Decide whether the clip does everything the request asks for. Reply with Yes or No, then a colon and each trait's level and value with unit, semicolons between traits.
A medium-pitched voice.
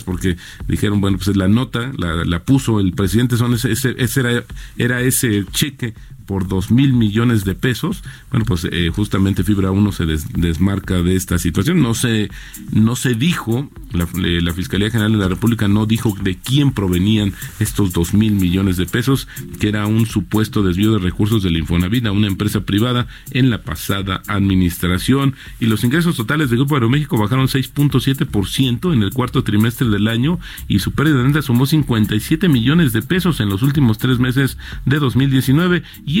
No: low, 110 Hz